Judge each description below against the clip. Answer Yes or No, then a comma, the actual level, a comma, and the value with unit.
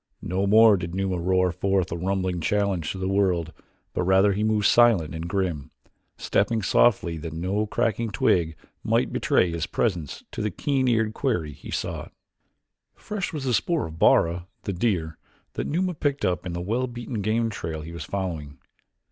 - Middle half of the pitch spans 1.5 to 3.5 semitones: No, average, 4.6 semitones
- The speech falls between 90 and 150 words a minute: No, average, 180 wpm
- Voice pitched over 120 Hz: No, very low, 95 Hz